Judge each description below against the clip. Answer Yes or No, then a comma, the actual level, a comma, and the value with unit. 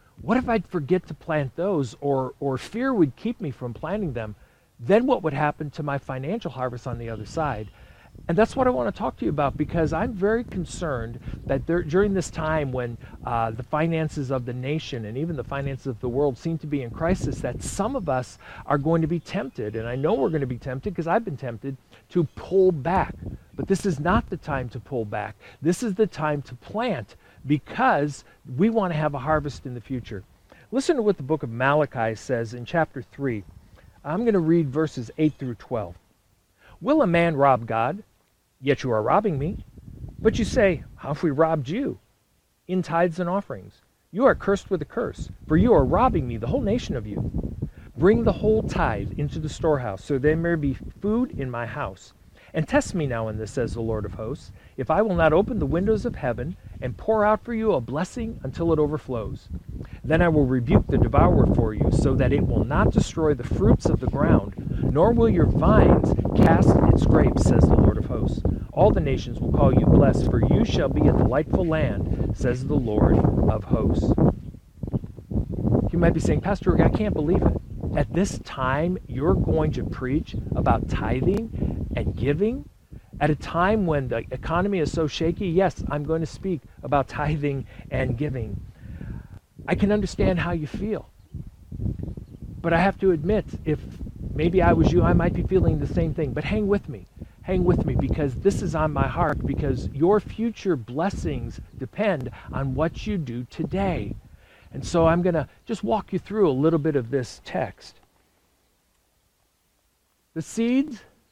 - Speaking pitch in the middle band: Yes, medium, 150 Hz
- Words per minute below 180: No, average, 200 wpm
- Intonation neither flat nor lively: No, wide, 6.3 semitones